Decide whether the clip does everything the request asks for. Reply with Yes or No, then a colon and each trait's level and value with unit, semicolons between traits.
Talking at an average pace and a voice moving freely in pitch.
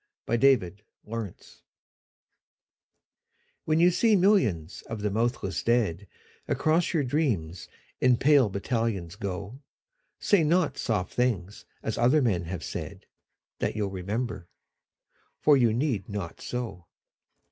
No: slow, 125 wpm; wide, 5.9 semitones